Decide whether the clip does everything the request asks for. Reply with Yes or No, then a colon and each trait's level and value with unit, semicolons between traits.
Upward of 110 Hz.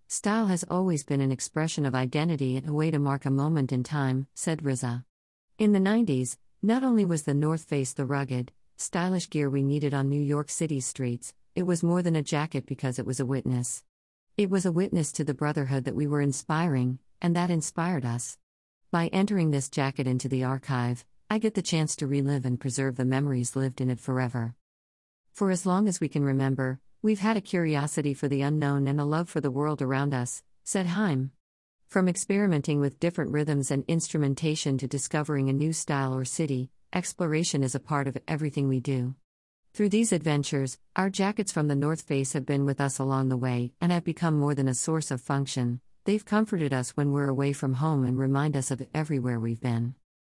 Yes: medium, 140 Hz